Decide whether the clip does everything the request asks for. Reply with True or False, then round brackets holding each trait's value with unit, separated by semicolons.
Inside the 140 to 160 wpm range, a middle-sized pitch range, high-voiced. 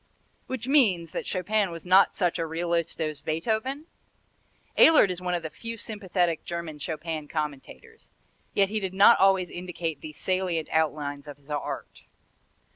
False (155 wpm; 3.9 semitones; 175 Hz)